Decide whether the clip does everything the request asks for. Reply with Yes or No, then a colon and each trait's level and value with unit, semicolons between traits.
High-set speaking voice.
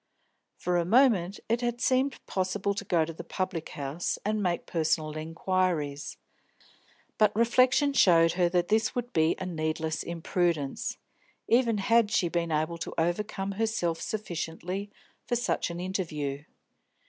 No: medium, 180 Hz